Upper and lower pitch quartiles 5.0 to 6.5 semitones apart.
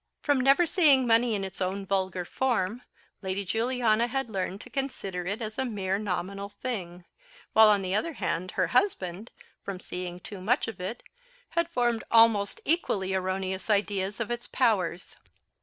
No: average, 4.4 semitones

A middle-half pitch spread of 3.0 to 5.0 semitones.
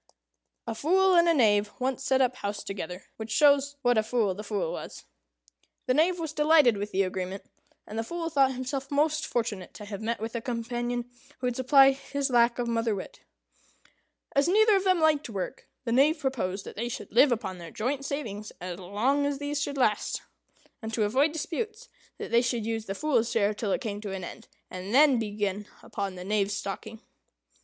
No: wide, 5.4 semitones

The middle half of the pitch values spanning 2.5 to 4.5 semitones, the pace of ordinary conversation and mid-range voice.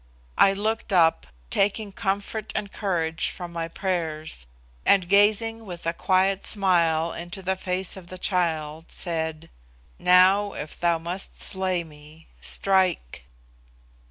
No: average, 3.1 semitones; slow, 130 wpm; medium, 180 Hz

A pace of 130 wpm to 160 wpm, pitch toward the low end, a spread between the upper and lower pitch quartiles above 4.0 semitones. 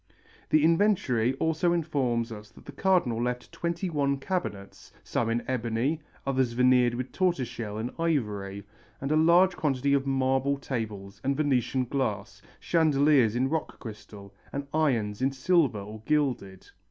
Yes: average, 150 wpm; low, 130 Hz; average, 5.0 semitones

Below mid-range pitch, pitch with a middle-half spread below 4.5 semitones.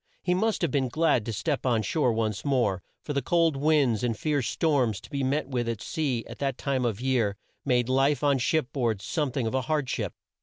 Yes: low, 130 Hz; average, 4.0 semitones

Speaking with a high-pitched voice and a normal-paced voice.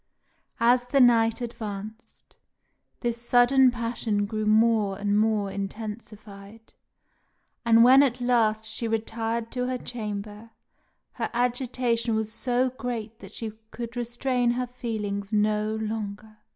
No: high, 225 Hz; slow, 125 wpm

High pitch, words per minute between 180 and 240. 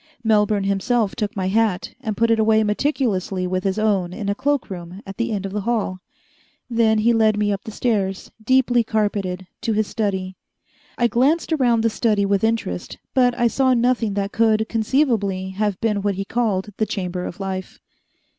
Yes: high, 215 Hz; average, 190 wpm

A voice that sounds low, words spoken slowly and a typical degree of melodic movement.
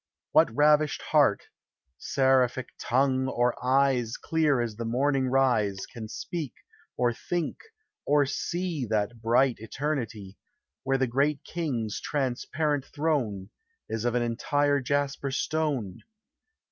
Yes: low, 130 Hz; slow, 120 wpm; average, 3.5 semitones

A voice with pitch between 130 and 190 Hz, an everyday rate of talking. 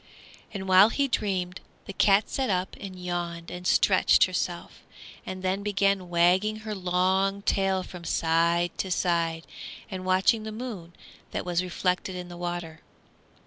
Yes: medium, 185 Hz; average, 150 wpm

